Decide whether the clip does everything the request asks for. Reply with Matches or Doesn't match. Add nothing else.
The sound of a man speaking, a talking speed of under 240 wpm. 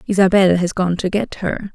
Doesn't match